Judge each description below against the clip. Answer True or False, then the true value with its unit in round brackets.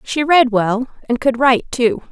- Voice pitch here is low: False (255 Hz)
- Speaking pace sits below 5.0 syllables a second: True (4.5 syllables/s)